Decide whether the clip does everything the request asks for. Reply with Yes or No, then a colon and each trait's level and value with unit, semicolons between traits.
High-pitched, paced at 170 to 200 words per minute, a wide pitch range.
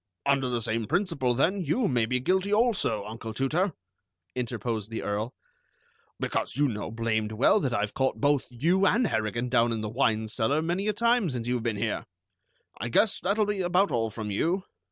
No: low, 125 Hz; average, 190 wpm; wide, 8.2 semitones